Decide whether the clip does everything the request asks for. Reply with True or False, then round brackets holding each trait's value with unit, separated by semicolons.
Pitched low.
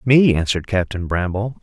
True (105 Hz)